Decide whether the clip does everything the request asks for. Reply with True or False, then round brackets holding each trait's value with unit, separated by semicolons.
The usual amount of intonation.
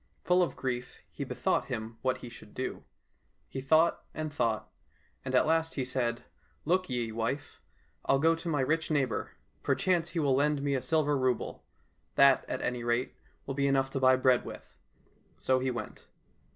True (3.5 semitones)